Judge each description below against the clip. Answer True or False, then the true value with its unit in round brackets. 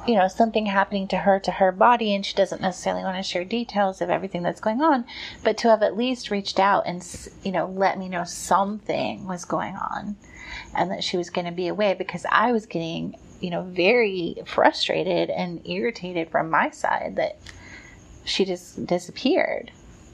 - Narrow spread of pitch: False (3.4 semitones)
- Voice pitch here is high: True (195 Hz)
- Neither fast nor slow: True (190 wpm)